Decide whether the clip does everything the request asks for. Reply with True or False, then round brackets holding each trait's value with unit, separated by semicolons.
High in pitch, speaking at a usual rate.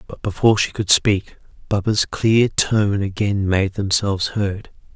False (100 Hz; 145 wpm)